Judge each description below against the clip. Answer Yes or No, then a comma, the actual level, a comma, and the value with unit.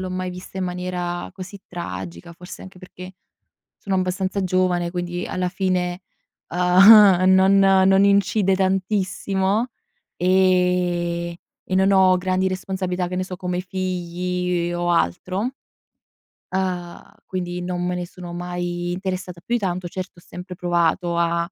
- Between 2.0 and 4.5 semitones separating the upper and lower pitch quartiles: No, narrow, 1.2 semitones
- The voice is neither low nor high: Yes, medium, 180 Hz